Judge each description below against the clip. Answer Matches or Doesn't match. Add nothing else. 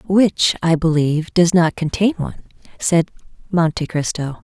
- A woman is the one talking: Matches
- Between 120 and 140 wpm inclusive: Matches